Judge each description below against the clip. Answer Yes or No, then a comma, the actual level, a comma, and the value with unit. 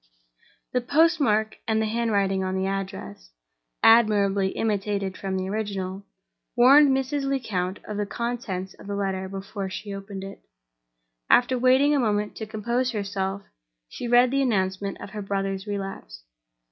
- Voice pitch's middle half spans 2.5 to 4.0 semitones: Yes, average, 3.5 semitones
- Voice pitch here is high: Yes, high, 205 Hz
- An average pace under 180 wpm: Yes, average, 145 wpm